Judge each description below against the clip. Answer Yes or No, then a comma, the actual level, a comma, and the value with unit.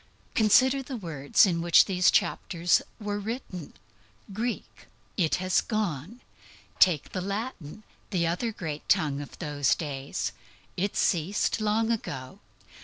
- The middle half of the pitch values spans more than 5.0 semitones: Yes, wide, 5.5 semitones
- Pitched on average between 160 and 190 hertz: Yes, medium, 185 Hz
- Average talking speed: No, slow, 125 wpm